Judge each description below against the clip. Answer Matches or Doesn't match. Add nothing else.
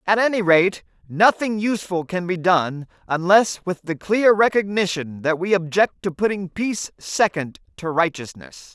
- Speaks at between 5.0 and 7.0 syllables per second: Doesn't match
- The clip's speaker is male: Matches